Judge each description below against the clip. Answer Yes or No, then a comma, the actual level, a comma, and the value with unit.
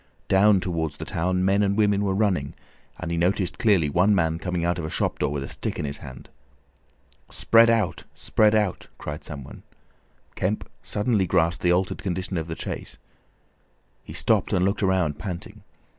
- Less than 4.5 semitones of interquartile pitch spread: Yes, average, 3.5 semitones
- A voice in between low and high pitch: No, very low, 90 Hz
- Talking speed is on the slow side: No, average, 185 wpm